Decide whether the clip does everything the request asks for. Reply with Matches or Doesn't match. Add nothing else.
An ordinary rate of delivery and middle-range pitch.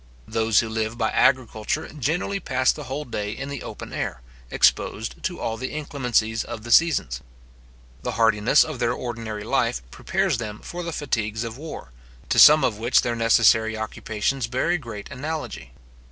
Doesn't match